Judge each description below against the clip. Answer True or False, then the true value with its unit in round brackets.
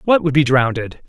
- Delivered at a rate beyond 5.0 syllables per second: True (5.3 syllables/s)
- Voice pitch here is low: False (145 Hz)